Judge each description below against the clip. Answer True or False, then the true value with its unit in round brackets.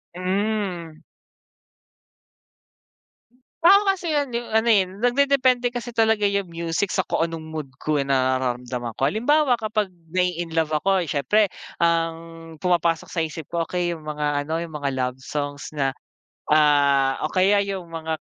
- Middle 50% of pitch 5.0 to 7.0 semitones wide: True (5.6 semitones)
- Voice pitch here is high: False (170 Hz)